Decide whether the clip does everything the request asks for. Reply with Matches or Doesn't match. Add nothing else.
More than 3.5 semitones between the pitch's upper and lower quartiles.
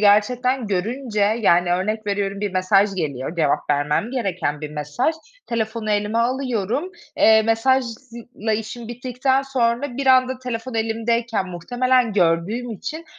Matches